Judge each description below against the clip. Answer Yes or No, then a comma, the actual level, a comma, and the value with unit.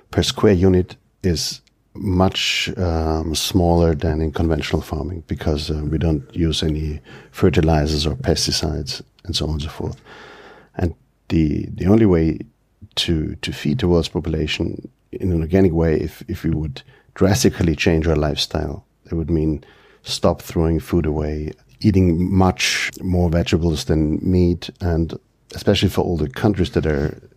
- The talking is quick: No, average, 155 wpm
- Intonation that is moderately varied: Yes, average, 3.2 semitones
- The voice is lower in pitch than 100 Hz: Yes, very low, 85 Hz